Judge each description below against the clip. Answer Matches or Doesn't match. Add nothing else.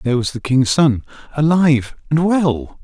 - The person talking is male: Matches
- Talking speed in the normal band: Matches